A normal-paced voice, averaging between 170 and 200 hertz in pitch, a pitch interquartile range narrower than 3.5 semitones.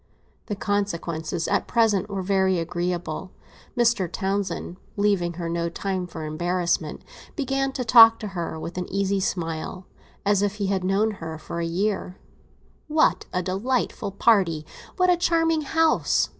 No: average, 145 wpm; high, 190 Hz; average, 3.8 semitones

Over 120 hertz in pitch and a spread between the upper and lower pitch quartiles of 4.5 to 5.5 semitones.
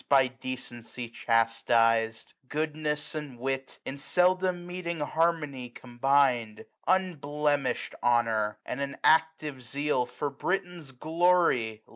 Yes: medium, 140 Hz; average, 4.9 semitones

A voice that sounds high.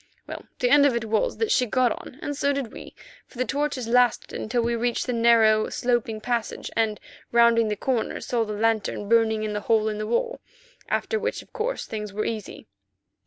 Yes: high, 235 Hz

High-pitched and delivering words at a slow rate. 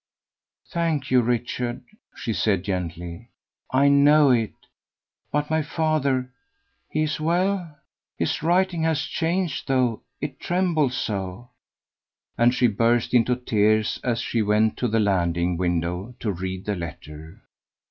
No: low, 120 Hz; slow, 130 wpm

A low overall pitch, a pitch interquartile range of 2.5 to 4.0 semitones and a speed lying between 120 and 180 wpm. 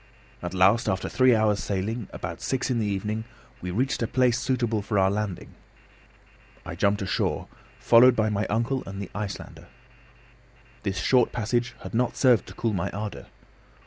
Yes: low, 110 Hz; average, 3.3 semitones; average, 170 wpm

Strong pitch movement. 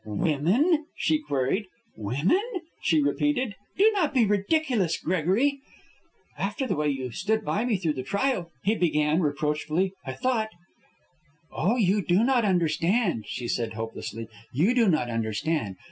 Yes: wide, 7.9 semitones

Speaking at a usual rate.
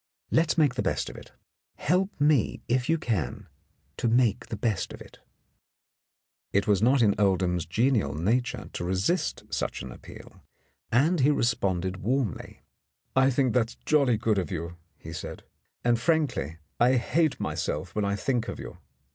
Yes: average, 165 wpm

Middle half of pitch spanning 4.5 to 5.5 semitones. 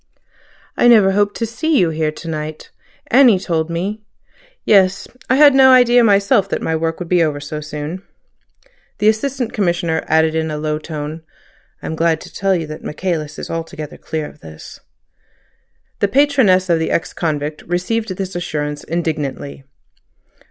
Yes: average, 4.8 semitones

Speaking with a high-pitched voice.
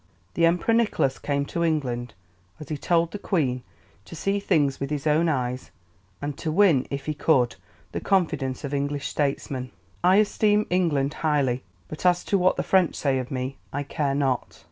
No: medium, 150 Hz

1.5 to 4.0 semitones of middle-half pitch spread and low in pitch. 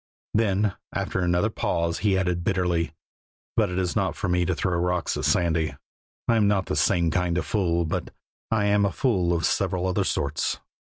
Yes: average, 2.7 semitones; very low, 90 Hz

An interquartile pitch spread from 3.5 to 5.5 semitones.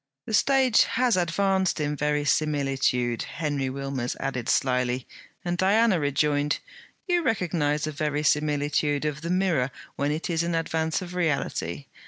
Yes: average, 3.9 semitones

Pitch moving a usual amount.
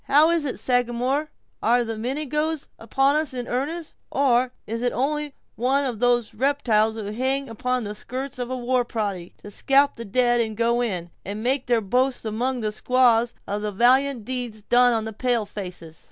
Yes: average, 3.2 semitones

